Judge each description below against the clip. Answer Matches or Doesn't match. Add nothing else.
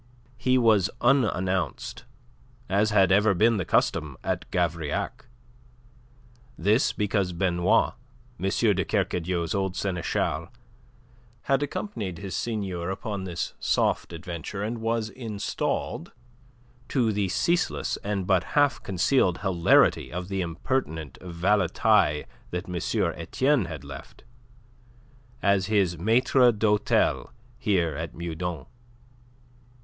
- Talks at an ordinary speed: Doesn't match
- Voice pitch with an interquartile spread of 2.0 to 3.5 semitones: Doesn't match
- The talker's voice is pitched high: Doesn't match